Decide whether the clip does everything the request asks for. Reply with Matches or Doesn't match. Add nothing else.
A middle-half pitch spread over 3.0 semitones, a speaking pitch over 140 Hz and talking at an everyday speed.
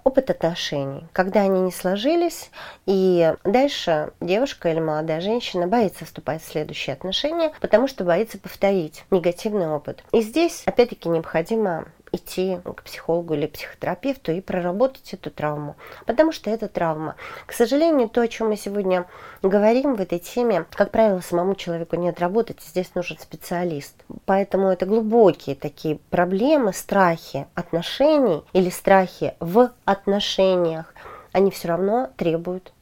Matches